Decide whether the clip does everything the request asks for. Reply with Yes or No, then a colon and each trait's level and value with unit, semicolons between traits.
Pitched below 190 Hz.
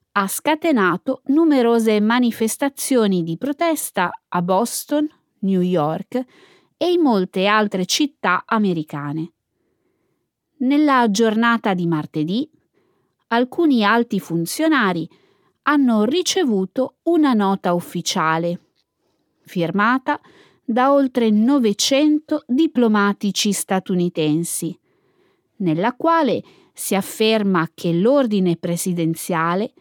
No: high, 220 Hz